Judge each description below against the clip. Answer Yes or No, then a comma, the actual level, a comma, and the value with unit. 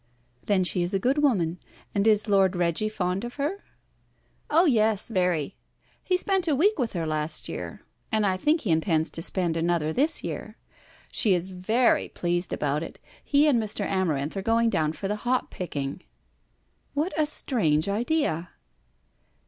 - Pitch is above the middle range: Yes, high, 195 Hz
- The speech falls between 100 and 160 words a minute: No, average, 170 wpm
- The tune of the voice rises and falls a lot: Yes, wide, 6.3 semitones